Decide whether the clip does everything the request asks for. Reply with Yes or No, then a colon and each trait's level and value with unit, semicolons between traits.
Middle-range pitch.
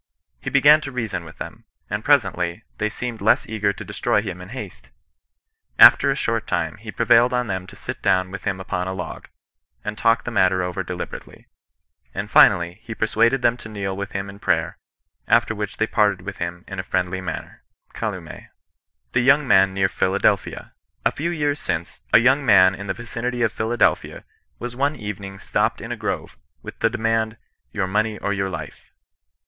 No: low, 105 Hz